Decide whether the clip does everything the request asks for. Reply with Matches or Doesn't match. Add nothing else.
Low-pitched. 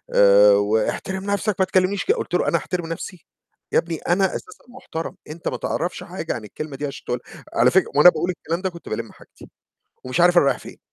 Doesn't match